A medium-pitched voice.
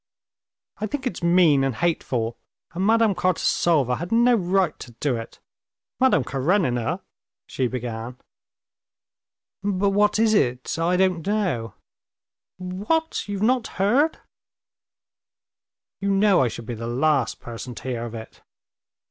Yes: medium, 175 Hz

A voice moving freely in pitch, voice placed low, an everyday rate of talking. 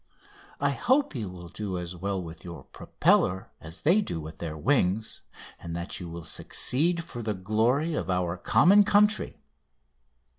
Yes: wide, 9.0 semitones; very low, 95 Hz; average, 160 wpm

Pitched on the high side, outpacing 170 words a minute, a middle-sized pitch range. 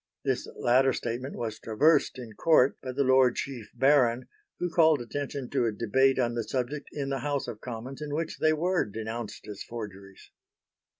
No: low, 130 Hz; average, 180 wpm; average, 3.5 semitones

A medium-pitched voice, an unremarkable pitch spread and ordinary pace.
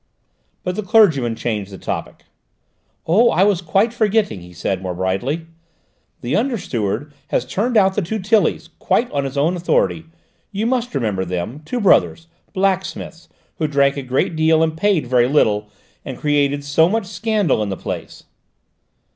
No: medium, 160 Hz; wide, 8.5 semitones; average, 165 wpm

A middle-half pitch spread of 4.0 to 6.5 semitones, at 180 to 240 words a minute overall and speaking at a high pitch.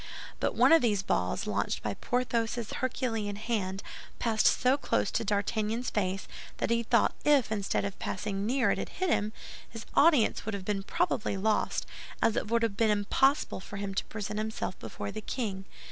No: average, 2.9 semitones; average, 190 wpm; high, 215 Hz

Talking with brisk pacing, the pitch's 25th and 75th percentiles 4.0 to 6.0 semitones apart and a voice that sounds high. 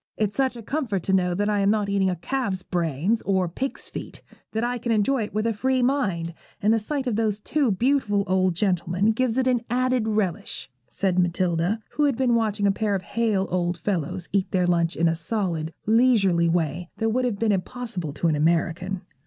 Yes: fast, 215 wpm; average, 4.6 semitones; high, 205 Hz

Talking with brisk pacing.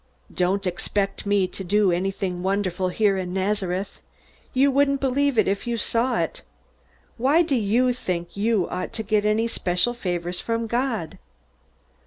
No: average, 155 wpm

